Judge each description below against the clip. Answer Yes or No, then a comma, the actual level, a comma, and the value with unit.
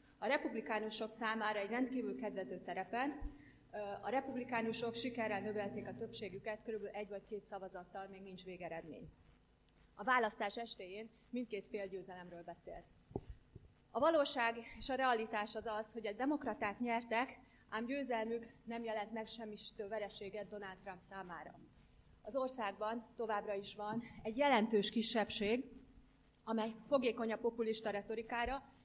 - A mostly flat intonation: Yes, narrow, 2.2 semitones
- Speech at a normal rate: Yes, average, 130 wpm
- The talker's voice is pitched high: Yes, high, 220 Hz